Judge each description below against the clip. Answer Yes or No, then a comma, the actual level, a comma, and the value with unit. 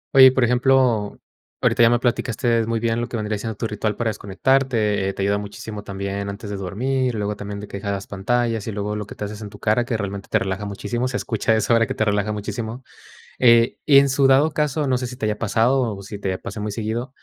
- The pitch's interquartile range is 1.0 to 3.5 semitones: Yes, average, 3.1 semitones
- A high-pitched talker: No, low, 110 Hz